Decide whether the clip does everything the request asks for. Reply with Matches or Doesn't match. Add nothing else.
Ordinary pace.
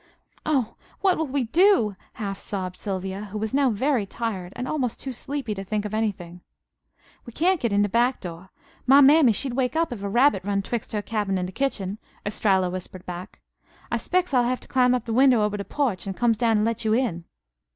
Doesn't match